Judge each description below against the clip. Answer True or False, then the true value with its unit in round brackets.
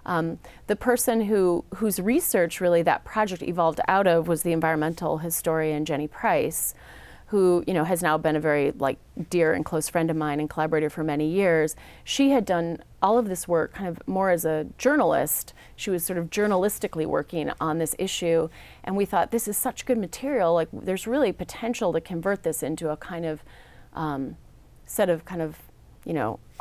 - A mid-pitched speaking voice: True (170 Hz)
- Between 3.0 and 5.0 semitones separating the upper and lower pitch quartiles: True (3.5 semitones)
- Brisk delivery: False (195 wpm)